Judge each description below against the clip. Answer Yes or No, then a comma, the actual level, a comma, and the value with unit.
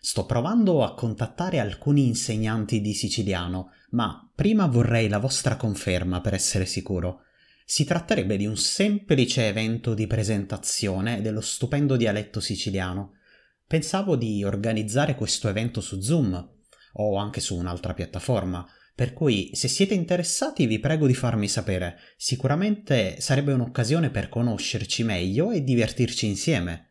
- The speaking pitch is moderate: No, low, 110 Hz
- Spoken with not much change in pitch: No, average, 5.3 semitones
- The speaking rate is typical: Yes, average, 135 wpm